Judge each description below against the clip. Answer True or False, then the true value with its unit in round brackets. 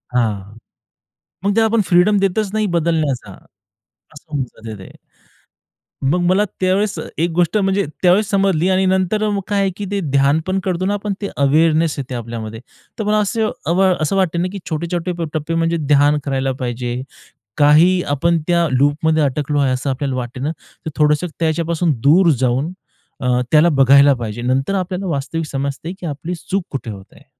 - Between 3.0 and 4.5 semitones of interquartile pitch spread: False (5.3 semitones)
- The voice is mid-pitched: True (160 Hz)